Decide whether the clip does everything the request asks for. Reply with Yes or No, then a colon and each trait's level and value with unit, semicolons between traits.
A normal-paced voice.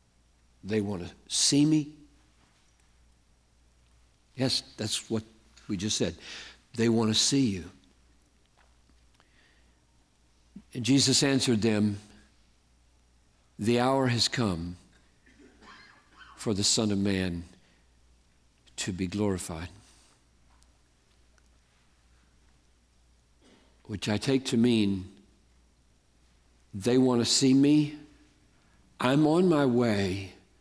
No: slow, 90 wpm